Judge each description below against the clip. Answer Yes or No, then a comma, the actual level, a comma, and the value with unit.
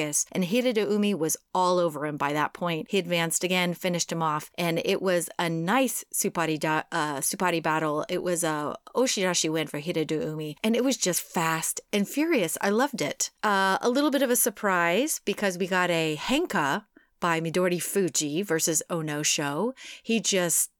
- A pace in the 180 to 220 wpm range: Yes, average, 185 wpm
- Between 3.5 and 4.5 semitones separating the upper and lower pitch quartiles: Yes, average, 3.9 semitones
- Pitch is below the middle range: No, medium, 175 Hz